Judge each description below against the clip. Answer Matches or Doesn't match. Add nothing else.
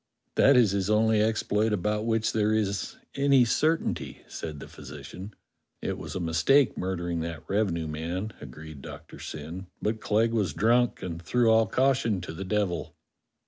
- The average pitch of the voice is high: Doesn't match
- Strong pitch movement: Doesn't match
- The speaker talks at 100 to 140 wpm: Doesn't match